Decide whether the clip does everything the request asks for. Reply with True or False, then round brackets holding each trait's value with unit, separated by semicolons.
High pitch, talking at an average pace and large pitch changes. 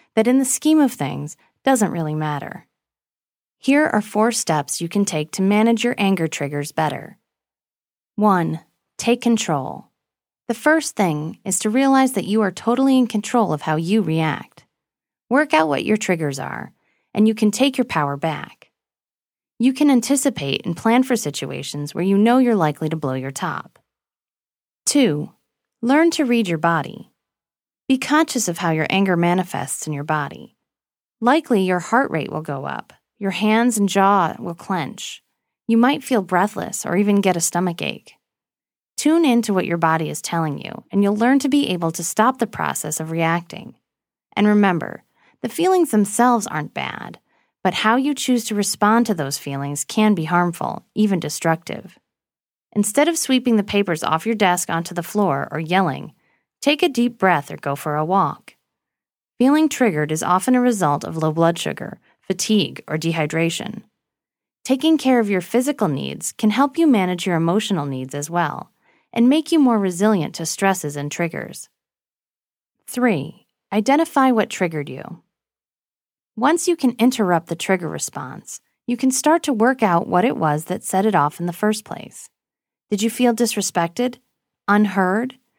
True (205 Hz; 170 wpm; 6.5 semitones)